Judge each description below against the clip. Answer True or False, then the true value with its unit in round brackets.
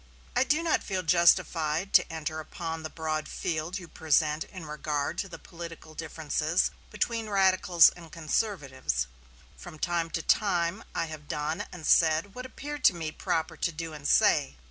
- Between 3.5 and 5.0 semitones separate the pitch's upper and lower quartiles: False (2.8 semitones)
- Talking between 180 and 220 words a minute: False (165 wpm)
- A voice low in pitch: False (165 Hz)